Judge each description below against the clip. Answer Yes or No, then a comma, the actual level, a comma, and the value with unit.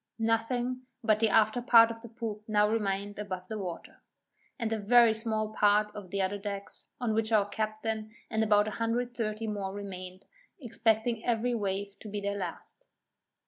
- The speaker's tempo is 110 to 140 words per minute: No, average, 165 wpm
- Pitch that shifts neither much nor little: No, narrow, 1.9 semitones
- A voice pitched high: Yes, high, 215 Hz